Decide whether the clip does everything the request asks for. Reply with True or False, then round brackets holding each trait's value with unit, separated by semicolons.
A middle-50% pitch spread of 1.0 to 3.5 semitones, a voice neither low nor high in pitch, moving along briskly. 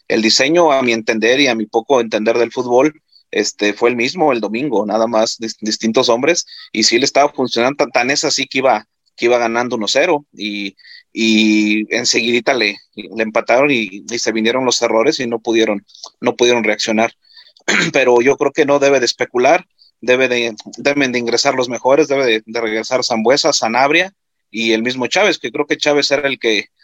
False (3.1 semitones; 120 Hz; 205 wpm)